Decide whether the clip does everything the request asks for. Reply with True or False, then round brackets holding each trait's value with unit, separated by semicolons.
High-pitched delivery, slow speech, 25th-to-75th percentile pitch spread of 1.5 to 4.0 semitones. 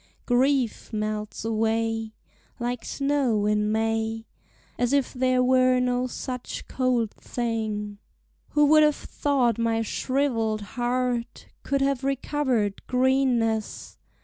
True (245 Hz; 110 wpm; 2.7 semitones)